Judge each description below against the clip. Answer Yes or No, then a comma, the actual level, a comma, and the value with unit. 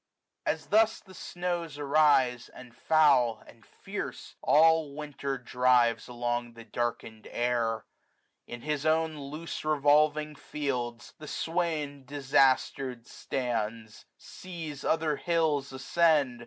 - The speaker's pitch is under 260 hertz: Yes, medium, 140 Hz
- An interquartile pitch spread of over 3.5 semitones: Yes, average, 4.3 semitones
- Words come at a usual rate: No, slow, 115 wpm